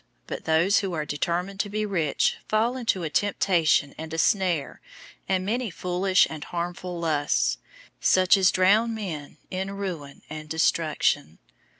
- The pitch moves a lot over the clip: No, average, 3.7 semitones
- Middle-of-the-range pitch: Yes, medium, 180 Hz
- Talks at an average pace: Yes, average, 155 wpm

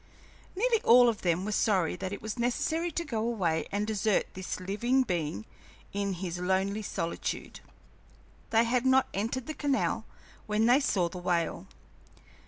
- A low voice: No, high, 210 Hz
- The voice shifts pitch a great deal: No, average, 5.0 semitones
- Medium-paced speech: Yes, average, 160 wpm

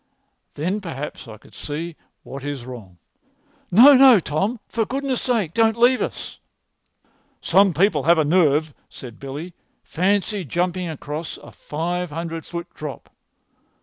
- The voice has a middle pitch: Yes, medium, 170 Hz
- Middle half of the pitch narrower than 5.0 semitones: No, wide, 5.4 semitones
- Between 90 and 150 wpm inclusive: Yes, average, 140 wpm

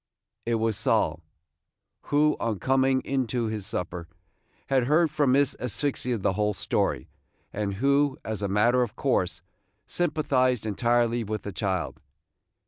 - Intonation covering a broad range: No, average, 4.2 semitones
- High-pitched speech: No, low, 120 Hz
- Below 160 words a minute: Yes, average, 140 wpm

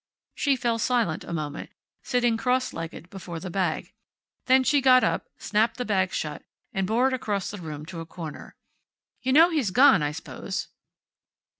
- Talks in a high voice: Yes, high, 210 Hz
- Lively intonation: Yes, wide, 7.1 semitones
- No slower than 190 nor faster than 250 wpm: No, average, 175 wpm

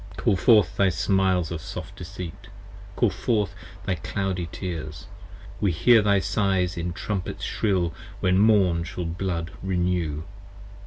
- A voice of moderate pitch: No, very low, 90 Hz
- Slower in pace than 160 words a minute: Yes, average, 140 wpm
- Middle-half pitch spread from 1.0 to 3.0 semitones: Yes, narrow, 2.6 semitones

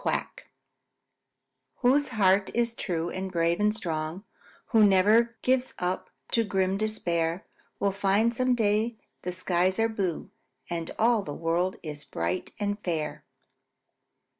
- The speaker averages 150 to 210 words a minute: No, slow, 135 wpm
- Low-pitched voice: No, high, 195 Hz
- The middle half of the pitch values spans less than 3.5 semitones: No, average, 4.4 semitones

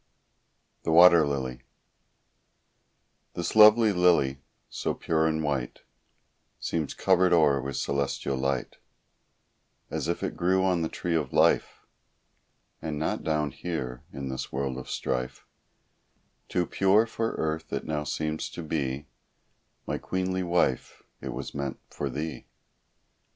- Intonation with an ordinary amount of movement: Yes, average, 4.3 semitones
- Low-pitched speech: Yes, very low, 80 Hz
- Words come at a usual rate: No, slow, 130 wpm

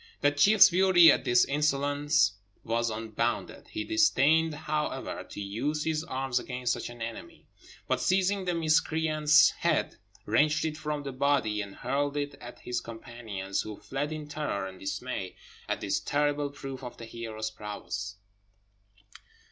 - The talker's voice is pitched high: No, medium, 140 Hz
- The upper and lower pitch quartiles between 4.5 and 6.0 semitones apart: Yes, average, 5.1 semitones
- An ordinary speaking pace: Yes, average, 150 wpm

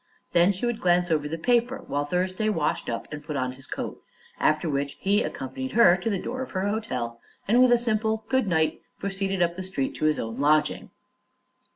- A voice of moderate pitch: Yes, medium, 180 Hz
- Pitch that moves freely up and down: Yes, wide, 6.6 semitones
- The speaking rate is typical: No, fast, 210 wpm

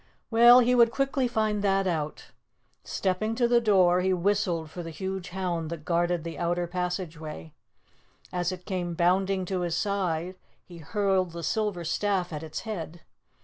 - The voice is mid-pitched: Yes, medium, 180 Hz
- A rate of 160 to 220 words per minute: Yes, average, 165 wpm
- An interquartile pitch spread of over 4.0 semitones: No, average, 3.0 semitones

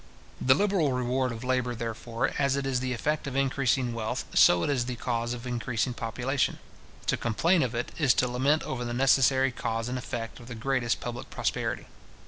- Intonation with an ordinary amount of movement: No, narrow, 2.1 semitones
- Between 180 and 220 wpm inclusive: Yes, average, 195 wpm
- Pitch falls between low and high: No, low, 125 Hz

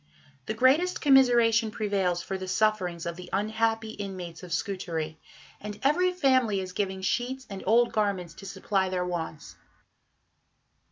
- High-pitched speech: Yes, high, 200 Hz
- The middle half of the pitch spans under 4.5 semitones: Yes, average, 4.0 semitones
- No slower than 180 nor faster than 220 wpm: No, average, 145 wpm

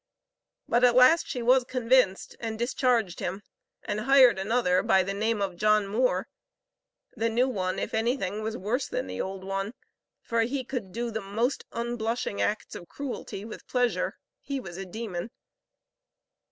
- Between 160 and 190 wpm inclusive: Yes, average, 165 wpm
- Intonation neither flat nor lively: Yes, average, 4.0 semitones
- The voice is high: Yes, high, 225 Hz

